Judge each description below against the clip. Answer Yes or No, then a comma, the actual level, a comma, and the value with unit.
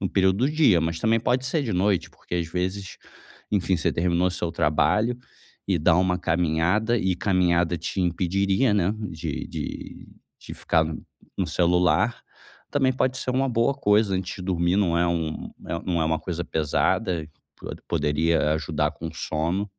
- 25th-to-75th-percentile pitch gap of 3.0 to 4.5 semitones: Yes, average, 3.8 semitones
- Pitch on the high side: No, very low, 90 Hz